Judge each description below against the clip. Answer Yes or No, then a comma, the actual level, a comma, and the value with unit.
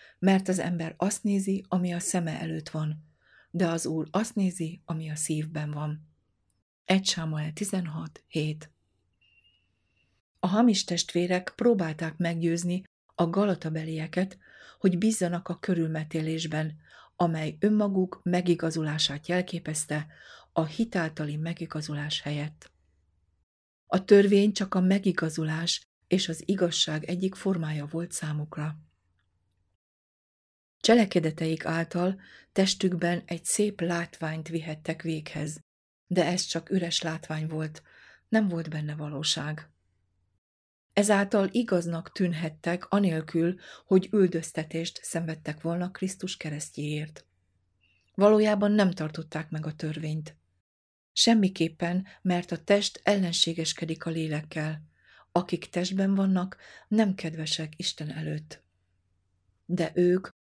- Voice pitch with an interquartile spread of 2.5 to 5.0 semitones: Yes, average, 3.0 semitones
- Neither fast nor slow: No, slow, 100 wpm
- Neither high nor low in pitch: Yes, medium, 165 Hz